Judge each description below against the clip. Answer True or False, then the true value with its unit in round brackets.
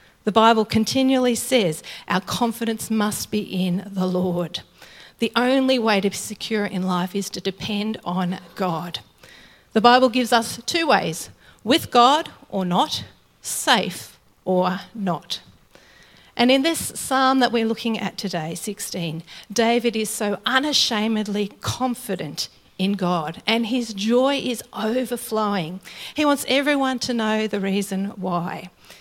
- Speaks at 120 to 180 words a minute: True (140 wpm)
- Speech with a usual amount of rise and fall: True (4.3 semitones)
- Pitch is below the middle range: False (215 Hz)